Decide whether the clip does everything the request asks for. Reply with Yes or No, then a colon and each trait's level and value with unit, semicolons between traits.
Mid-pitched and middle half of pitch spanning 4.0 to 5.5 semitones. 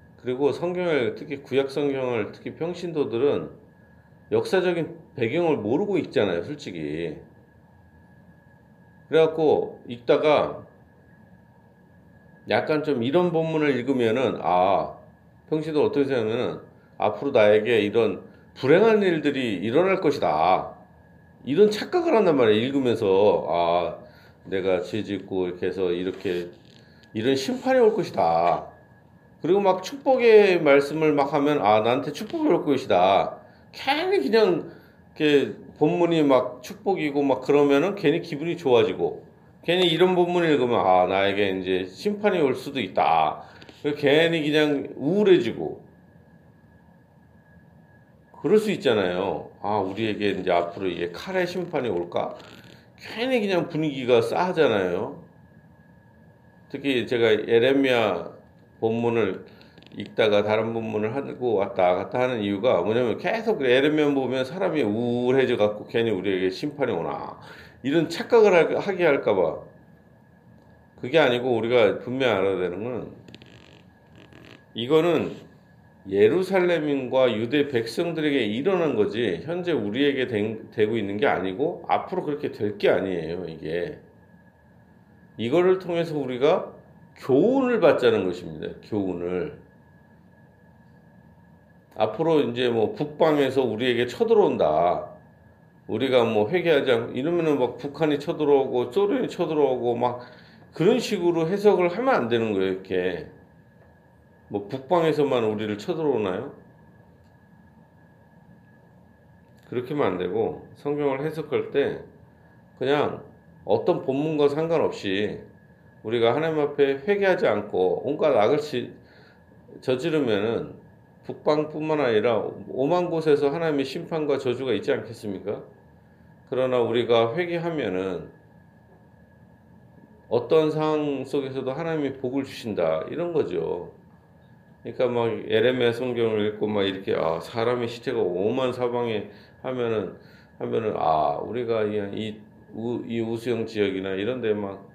No: medium, 145 Hz; wide, 7.1 semitones